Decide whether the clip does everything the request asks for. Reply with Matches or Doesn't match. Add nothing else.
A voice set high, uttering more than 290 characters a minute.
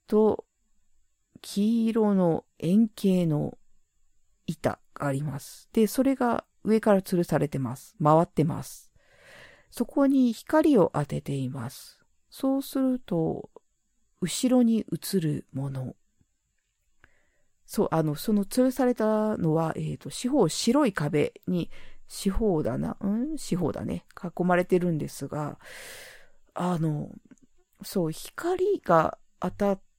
Doesn't match